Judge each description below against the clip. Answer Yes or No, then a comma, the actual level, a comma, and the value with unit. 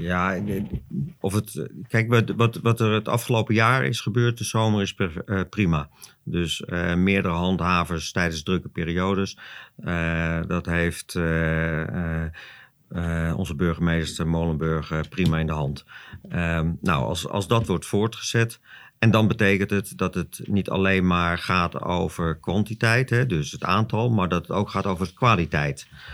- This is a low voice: Yes, very low, 90 Hz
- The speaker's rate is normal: Yes, average, 150 wpm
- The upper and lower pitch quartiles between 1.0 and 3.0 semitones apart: No, average, 4.2 semitones